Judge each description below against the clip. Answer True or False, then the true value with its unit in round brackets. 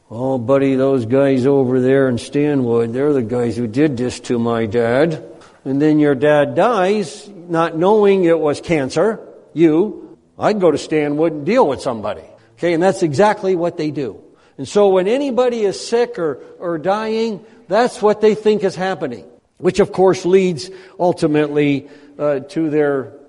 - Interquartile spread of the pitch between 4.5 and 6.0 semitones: True (5.5 semitones)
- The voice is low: False (155 Hz)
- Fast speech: False (170 wpm)